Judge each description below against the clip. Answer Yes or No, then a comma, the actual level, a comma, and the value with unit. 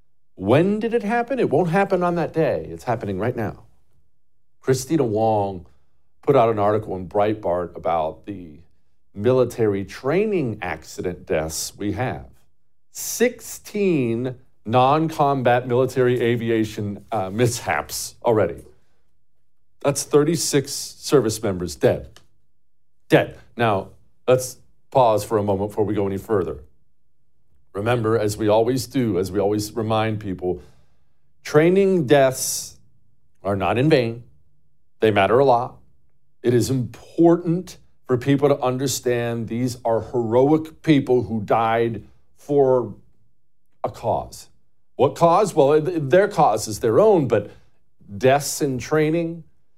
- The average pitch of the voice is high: No, low, 120 Hz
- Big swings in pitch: Yes, wide, 5.8 semitones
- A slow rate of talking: Yes, slow, 125 wpm